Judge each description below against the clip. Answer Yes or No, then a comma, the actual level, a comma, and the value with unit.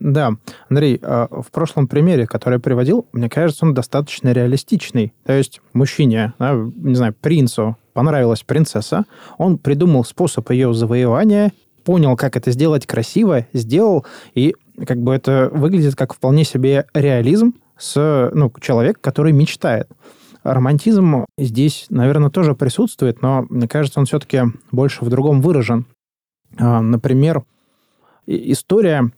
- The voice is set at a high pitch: No, low, 135 Hz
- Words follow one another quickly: No, average, 125 wpm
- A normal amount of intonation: Yes, average, 3.5 semitones